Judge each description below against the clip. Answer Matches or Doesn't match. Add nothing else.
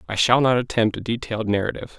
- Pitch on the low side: Matches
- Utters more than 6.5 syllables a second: Matches